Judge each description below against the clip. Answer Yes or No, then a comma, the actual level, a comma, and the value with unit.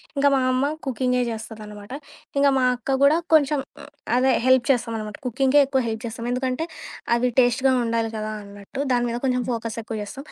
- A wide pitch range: No, average, 2.9 semitones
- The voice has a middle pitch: No, high, 245 Hz